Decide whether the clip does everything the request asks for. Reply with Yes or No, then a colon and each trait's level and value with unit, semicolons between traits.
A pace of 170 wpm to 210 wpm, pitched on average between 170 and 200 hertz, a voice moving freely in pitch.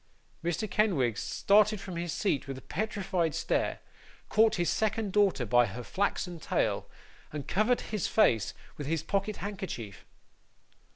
No: average, 140 wpm; medium, 185 Hz; wide, 6.4 semitones